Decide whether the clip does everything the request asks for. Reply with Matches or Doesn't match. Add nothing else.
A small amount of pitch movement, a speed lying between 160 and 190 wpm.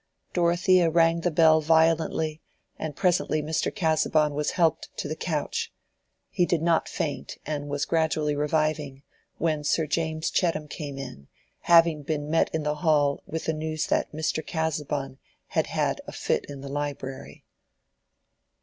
Doesn't match